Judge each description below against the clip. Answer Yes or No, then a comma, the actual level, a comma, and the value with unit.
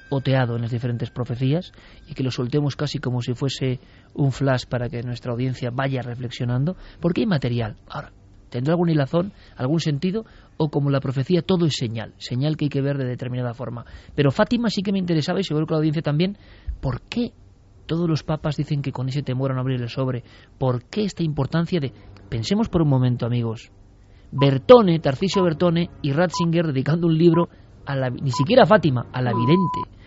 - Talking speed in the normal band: No, fast, 195 wpm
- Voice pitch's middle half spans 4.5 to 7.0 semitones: Yes, average, 5.1 semitones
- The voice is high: No, low, 135 Hz